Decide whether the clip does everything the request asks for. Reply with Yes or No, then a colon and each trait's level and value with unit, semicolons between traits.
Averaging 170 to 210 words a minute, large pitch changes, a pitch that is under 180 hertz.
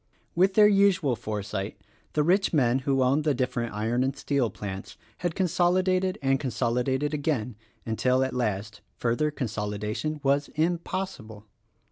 No: average, 140 wpm; wide, 5.8 semitones; low, 135 Hz